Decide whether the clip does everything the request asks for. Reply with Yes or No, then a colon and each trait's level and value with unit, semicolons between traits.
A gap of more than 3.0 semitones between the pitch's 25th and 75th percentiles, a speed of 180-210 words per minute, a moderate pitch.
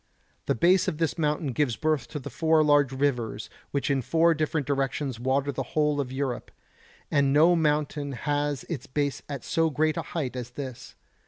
No: narrow, 2.6 semitones; average, 185 wpm; medium, 145 Hz